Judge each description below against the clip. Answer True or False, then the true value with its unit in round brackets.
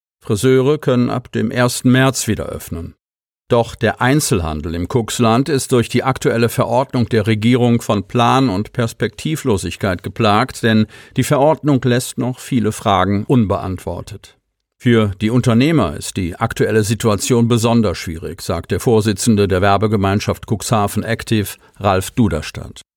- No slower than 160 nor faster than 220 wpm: False (135 wpm)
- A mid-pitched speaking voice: False (115 Hz)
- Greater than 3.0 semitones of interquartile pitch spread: True (3.4 semitones)